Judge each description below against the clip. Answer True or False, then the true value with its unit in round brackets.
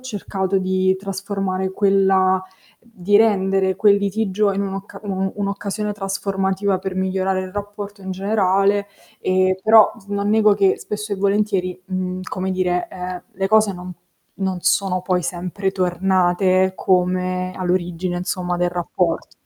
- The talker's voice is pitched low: False (190 Hz)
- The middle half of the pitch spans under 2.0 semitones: True (1.5 semitones)